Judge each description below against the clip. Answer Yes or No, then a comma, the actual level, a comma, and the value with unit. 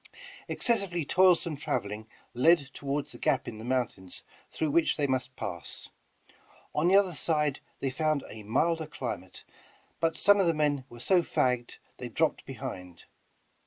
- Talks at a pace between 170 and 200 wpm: No, average, 155 wpm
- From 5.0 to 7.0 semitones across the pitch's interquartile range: Yes, average, 5.3 semitones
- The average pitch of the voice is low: No, medium, 145 Hz